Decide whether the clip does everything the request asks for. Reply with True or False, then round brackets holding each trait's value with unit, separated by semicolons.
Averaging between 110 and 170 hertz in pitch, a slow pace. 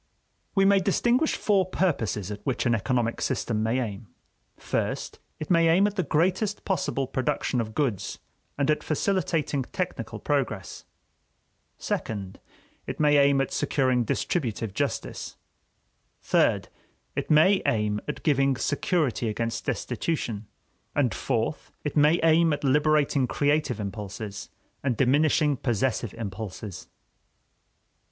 True (135 Hz; 125 wpm)